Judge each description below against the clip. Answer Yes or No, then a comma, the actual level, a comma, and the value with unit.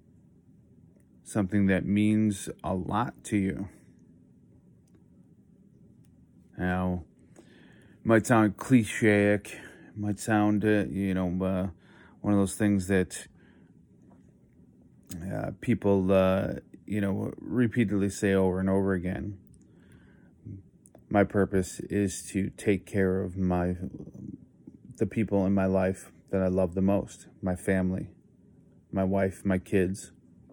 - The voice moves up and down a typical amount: No, narrow, 1.7 semitones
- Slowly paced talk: Yes, slow, 115 wpm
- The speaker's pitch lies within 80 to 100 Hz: Yes, very low, 95 Hz